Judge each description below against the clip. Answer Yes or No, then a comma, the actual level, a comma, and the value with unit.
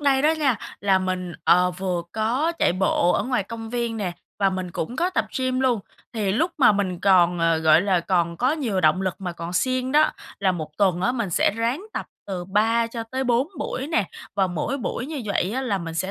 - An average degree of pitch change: No, wide, 5.8 semitones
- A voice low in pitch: No, high, 205 Hz